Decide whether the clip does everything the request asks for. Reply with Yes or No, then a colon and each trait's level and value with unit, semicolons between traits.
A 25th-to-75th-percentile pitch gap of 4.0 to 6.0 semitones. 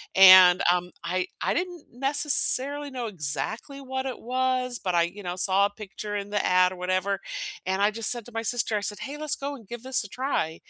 Yes: wide, 5.6 semitones